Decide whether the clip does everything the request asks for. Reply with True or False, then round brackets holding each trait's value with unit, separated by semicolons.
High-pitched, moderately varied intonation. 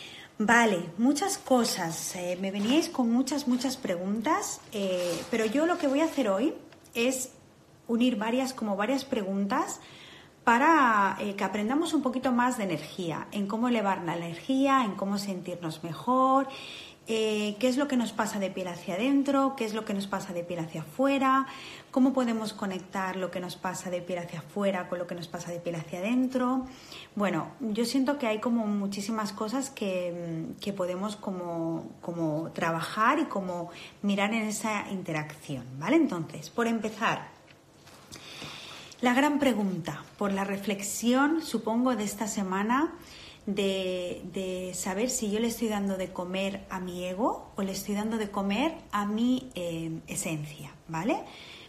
False (205 Hz; 5.8 semitones)